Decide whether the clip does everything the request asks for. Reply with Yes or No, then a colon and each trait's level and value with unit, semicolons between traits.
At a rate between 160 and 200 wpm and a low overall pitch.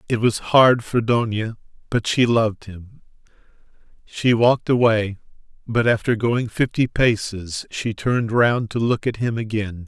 No: average, 150 wpm; low, 115 Hz